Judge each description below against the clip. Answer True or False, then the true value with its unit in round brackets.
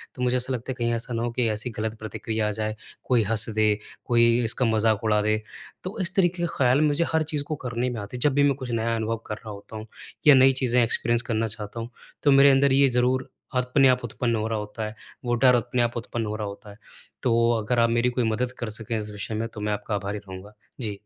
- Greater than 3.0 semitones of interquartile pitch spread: False (2.7 semitones)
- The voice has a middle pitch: False (115 Hz)